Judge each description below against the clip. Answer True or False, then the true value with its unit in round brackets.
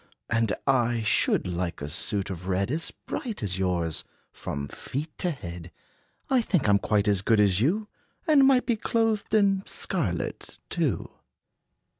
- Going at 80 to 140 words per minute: False (160 wpm)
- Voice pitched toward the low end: True (110 Hz)